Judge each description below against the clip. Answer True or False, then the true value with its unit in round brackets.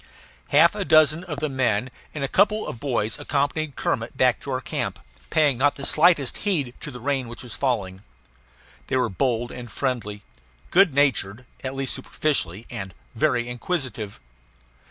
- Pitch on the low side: True (130 Hz)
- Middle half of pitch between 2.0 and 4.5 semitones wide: True (3.8 semitones)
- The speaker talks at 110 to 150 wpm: False (160 wpm)